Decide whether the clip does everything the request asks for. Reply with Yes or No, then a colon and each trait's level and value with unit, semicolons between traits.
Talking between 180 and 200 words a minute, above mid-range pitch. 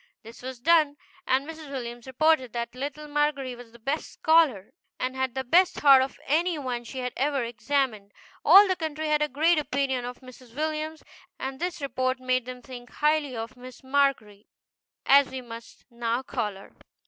Yes: average, 185 wpm; very high, 265 Hz